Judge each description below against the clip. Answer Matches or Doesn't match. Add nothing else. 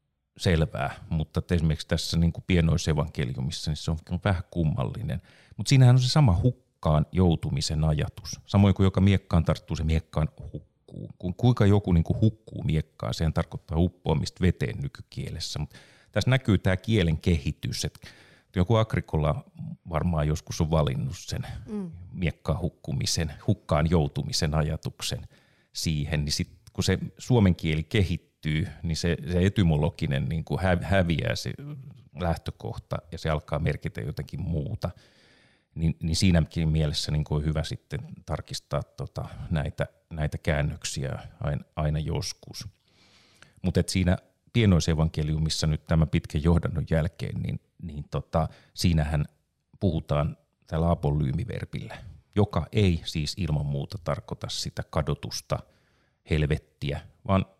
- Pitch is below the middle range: Matches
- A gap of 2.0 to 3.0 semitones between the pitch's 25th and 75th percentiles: Doesn't match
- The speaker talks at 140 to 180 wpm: Doesn't match